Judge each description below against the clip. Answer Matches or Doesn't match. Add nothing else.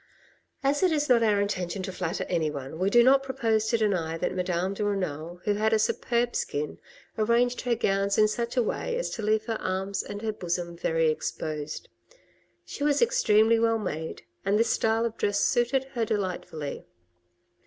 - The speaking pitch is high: Matches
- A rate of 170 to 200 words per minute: Matches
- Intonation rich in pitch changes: Doesn't match